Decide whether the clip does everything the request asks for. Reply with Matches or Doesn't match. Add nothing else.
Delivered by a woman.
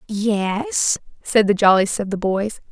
Matches